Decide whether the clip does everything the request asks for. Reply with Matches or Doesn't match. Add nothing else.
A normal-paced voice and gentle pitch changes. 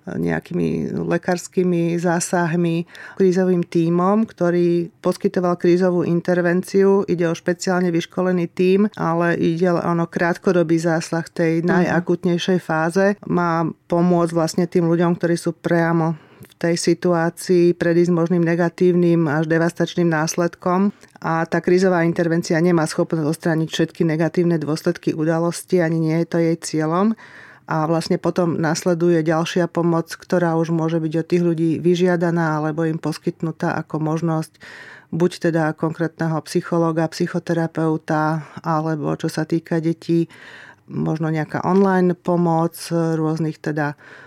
Matches